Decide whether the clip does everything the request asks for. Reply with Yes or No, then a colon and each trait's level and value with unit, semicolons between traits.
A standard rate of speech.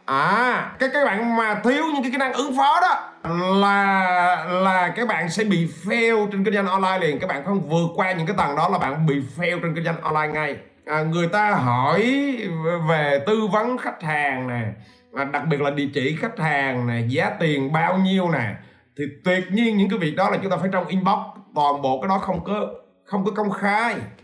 Yes: average, 225 wpm